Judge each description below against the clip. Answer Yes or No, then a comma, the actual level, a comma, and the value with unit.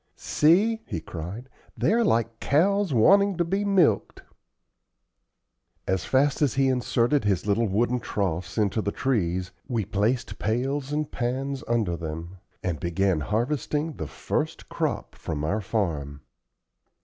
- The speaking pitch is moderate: No, low, 115 Hz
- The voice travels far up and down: Yes, wide, 7.3 semitones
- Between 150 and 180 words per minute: No, slow, 135 wpm